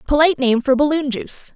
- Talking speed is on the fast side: Yes, fast, 230 wpm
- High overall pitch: Yes, very high, 280 Hz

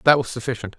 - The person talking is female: No, male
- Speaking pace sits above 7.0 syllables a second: Yes, 7.5 syllables/s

